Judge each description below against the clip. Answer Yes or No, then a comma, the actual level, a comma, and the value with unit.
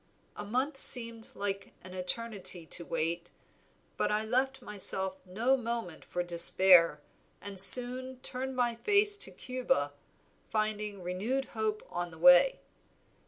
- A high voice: Yes, high, 215 Hz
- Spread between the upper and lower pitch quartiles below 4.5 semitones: No, wide, 5.6 semitones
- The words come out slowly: Yes, slow, 125 wpm